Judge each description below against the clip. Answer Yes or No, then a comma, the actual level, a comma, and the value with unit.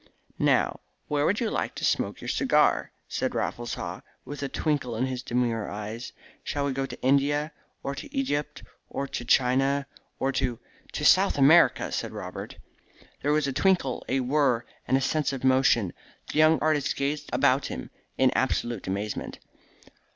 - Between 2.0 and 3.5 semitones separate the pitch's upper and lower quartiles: Yes, average, 2.9 semitones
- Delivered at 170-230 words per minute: Yes, average, 175 wpm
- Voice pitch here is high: No, low, 135 Hz